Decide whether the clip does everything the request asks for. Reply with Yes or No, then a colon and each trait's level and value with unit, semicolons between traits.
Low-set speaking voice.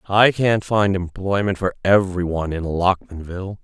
Yes: very low, 95 Hz